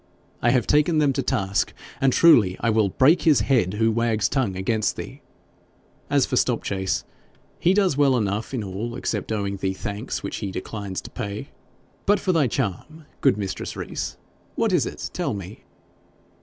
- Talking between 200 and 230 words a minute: No, average, 175 wpm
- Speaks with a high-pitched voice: No, low, 110 Hz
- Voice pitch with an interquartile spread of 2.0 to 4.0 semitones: No, average, 5.3 semitones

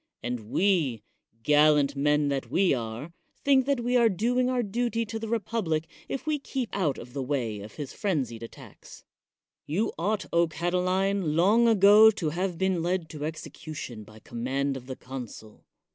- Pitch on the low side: No, medium, 170 Hz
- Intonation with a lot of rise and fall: Yes, wide, 7.5 semitones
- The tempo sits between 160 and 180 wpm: Yes, average, 170 wpm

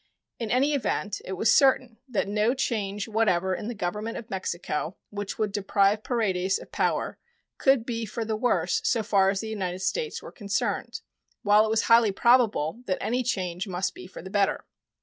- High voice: Yes, high, 210 Hz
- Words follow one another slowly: No, average, 190 wpm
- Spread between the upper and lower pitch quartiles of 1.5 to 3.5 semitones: Yes, average, 3.2 semitones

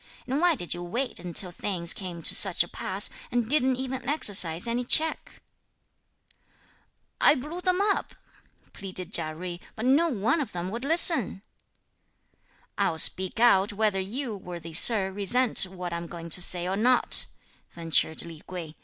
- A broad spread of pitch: Yes, wide, 6.4 semitones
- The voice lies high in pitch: Yes, high, 195 Hz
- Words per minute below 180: Yes, average, 160 wpm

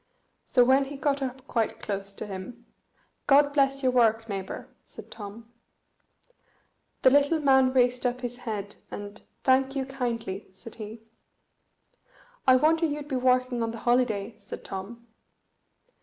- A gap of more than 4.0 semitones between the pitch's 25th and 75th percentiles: No, average, 3.3 semitones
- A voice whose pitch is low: No, very high, 250 Hz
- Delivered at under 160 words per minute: Yes, average, 145 wpm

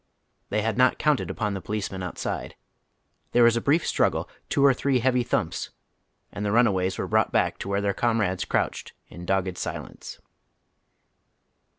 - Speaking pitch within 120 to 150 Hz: No, low, 105 Hz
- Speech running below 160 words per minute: No, average, 165 wpm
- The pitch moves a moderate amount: Yes, average, 4.2 semitones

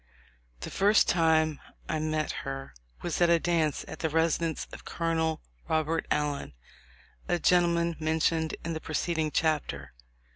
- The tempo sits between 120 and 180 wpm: Yes, average, 140 wpm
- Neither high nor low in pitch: Yes, medium, 160 Hz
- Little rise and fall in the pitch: Yes, narrow, 1.5 semitones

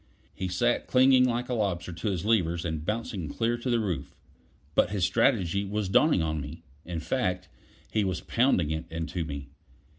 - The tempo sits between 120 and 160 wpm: No, average, 180 wpm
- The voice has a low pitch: Yes, very low, 95 Hz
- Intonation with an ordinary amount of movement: No, wide, 5.8 semitones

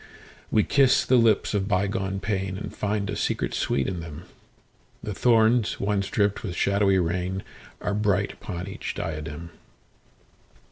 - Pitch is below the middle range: Yes, low, 100 Hz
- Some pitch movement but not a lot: No, narrow, 2.2 semitones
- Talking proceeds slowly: Yes, slow, 130 wpm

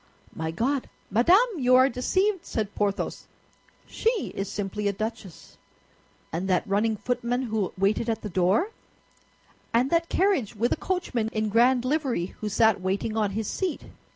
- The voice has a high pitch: Yes, high, 225 Hz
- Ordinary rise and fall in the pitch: Yes, average, 4.4 semitones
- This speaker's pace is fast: No, average, 155 wpm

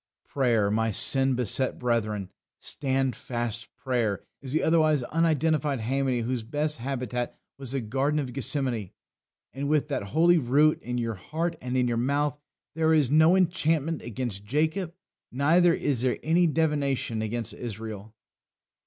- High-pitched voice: No, low, 135 Hz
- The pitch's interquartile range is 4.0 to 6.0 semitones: Yes, average, 4.4 semitones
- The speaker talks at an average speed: Yes, average, 145 wpm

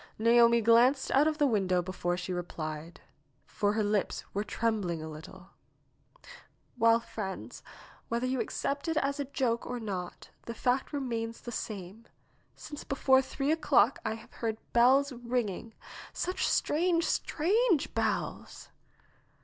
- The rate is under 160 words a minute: Yes, average, 140 wpm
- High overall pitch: Yes, high, 235 Hz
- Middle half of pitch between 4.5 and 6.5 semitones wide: Yes, average, 5.1 semitones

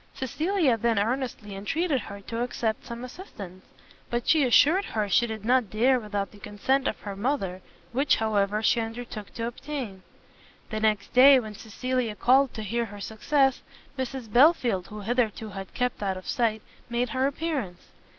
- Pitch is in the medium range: No, high, 235 Hz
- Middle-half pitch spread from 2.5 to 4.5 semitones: Yes, average, 3.8 semitones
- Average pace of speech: Yes, average, 170 wpm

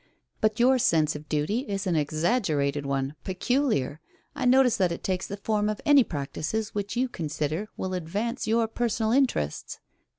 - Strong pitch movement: Yes, wide, 7.2 semitones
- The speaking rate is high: No, average, 165 wpm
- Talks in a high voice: Yes, high, 200 Hz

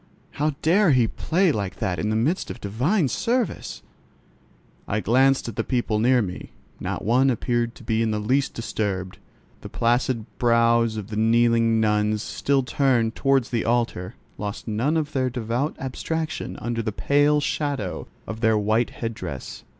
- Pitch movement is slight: No, average, 3.8 semitones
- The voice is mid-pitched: No, low, 115 Hz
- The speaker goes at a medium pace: Yes, average, 165 wpm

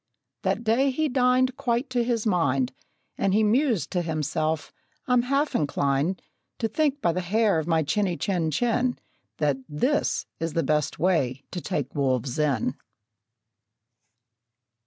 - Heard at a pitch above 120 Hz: Yes, medium, 185 Hz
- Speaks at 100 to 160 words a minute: Yes, average, 145 wpm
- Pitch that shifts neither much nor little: No, wide, 8.3 semitones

